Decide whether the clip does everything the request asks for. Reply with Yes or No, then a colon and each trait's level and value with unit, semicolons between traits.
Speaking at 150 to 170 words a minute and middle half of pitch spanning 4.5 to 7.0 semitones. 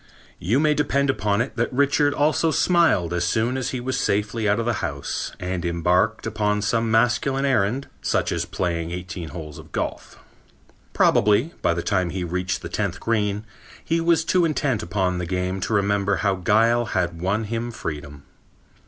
No: average, 180 wpm; average, 5.2 semitones